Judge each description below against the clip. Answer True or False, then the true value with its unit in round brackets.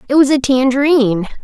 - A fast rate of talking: False (165 wpm)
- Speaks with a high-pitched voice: True (265 Hz)